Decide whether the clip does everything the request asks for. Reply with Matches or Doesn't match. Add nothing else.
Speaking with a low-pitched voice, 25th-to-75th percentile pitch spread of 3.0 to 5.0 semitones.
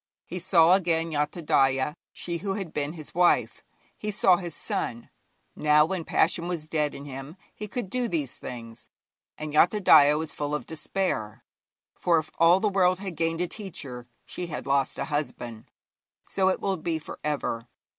Doesn't match